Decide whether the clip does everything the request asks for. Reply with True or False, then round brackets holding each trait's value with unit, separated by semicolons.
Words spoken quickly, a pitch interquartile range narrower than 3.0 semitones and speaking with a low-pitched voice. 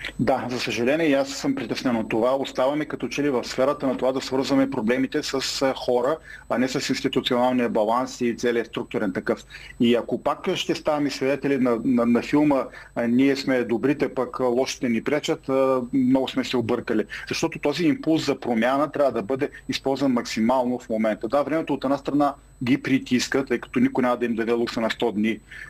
True (195 wpm; 2.6 semitones; 130 Hz)